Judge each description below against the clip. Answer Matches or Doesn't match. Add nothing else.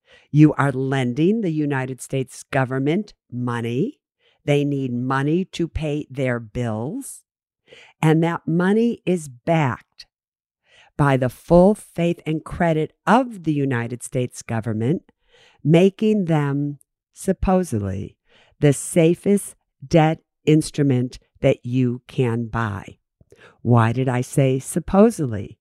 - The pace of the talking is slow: Matches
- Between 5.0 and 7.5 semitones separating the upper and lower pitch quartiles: Matches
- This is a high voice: Doesn't match